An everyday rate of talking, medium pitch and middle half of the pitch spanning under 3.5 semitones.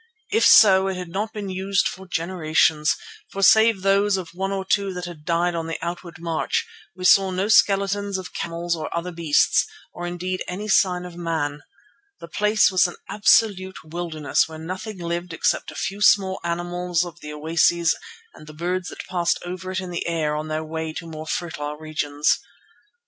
Yes: average, 185 wpm; medium, 175 Hz; average, 2.7 semitones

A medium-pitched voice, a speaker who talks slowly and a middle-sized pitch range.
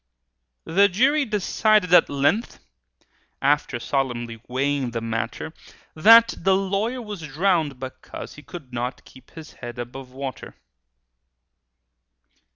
No: medium, 150 Hz; slow, 115 wpm; wide, 7.5 semitones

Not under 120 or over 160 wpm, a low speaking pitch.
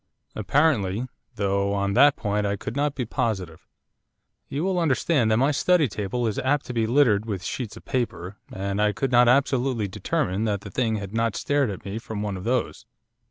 No: average, 200 wpm; low, 115 Hz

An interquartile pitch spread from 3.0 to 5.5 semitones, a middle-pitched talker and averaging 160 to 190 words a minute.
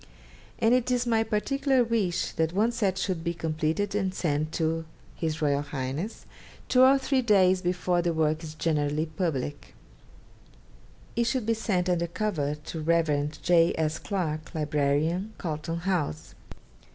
No: average, 5.2 semitones; medium, 170 Hz; average, 145 wpm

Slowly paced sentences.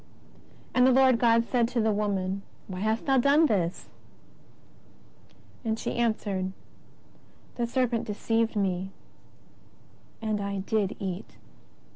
Yes: slow, 120 wpm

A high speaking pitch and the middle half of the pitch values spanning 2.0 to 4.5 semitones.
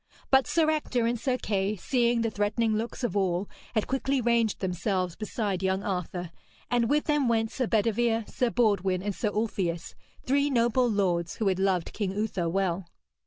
Yes: high, 215 Hz; average, 3.9 semitones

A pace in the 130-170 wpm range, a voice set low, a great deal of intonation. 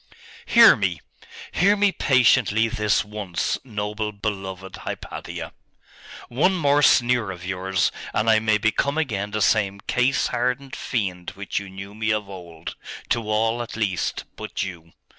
No: average, 145 wpm; low, 105 Hz; average, 3.8 semitones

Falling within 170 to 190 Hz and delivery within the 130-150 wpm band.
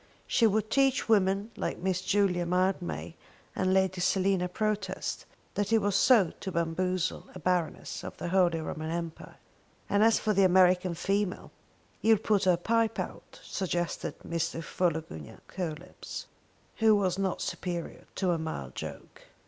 Yes: medium, 185 Hz; average, 145 wpm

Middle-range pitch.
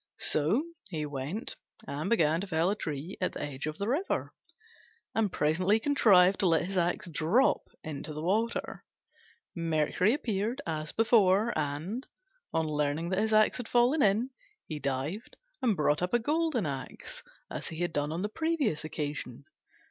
Yes: medium, 180 Hz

